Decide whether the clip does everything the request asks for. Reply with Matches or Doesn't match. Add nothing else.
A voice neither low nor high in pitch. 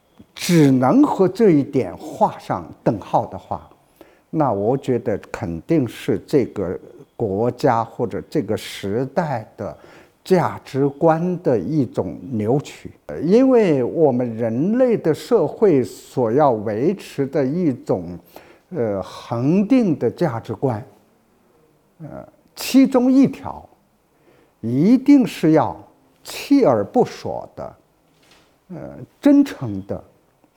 Matches